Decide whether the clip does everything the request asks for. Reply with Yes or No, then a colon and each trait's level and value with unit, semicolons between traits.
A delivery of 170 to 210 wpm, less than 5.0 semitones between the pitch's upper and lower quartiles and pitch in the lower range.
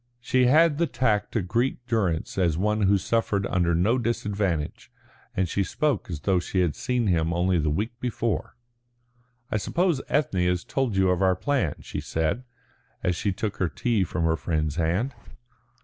No: average, 180 wpm; wide, 5.4 semitones; low, 100 Hz